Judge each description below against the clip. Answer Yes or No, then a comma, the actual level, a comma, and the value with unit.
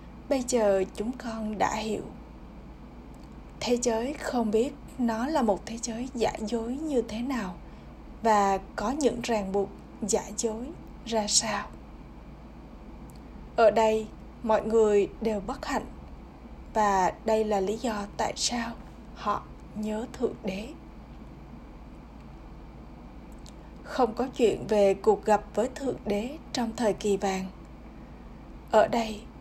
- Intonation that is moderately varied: No, narrow, 2.3 semitones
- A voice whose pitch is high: Yes, high, 220 Hz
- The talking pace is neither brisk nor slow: No, slow, 125 wpm